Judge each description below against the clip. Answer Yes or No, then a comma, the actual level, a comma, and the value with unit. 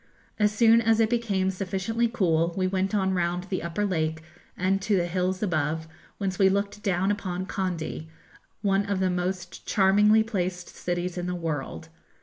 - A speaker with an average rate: Yes, average, 170 wpm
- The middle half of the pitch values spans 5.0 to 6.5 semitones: No, narrow, 2.4 semitones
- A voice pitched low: No, high, 190 Hz